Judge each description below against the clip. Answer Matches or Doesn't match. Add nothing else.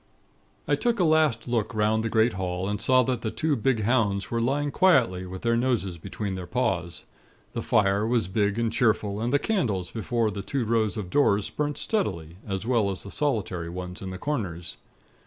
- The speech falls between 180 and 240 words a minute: Matches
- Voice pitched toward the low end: Matches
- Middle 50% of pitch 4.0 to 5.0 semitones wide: Matches